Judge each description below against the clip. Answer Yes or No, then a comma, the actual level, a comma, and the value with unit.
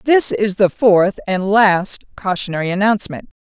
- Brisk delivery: No, average, 140 wpm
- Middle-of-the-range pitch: No, high, 205 Hz